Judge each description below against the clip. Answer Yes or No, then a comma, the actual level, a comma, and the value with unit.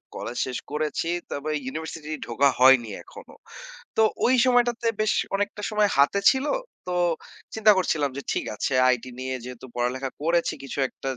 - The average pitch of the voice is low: No, medium, 150 Hz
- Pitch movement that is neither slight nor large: No, wide, 7.7 semitones